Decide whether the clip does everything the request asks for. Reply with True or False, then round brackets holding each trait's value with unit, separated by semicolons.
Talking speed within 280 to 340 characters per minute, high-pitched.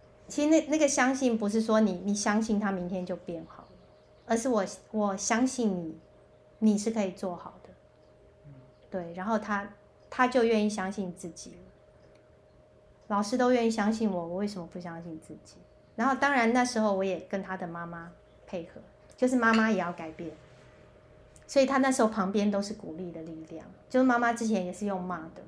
False (265 characters per minute; 205 Hz)